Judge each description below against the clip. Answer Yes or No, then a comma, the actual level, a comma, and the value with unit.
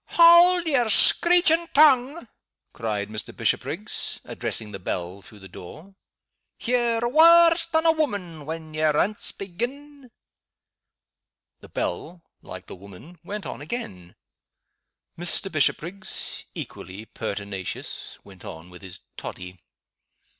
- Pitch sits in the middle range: Yes, medium, 175 Hz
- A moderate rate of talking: No, slow, 115 wpm